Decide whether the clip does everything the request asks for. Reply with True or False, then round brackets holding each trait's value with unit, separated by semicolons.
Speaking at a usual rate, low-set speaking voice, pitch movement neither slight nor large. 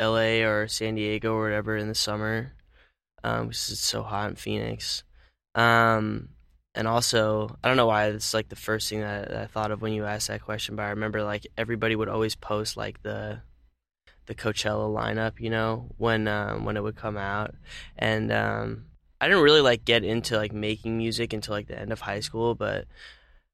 False (195 wpm; 110 Hz; 1.2 semitones)